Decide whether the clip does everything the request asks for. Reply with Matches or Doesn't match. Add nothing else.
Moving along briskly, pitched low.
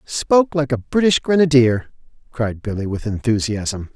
Doesn't match